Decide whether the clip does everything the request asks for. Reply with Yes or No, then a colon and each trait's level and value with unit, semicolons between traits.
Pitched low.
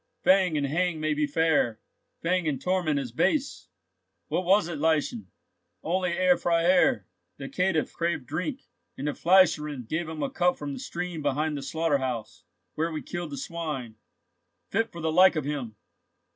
No: medium, 160 Hz